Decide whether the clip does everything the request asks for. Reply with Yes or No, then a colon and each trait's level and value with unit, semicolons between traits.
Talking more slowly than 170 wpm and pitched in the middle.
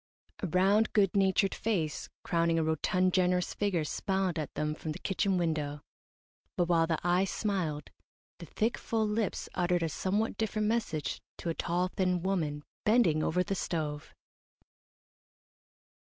Yes: average, 150 wpm; medium, 180 Hz